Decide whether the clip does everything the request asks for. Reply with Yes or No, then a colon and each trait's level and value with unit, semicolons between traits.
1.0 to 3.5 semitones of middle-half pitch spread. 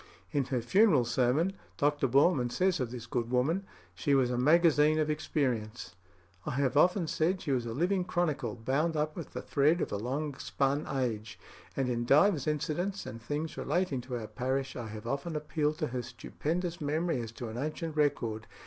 No: average, 4.4 semitones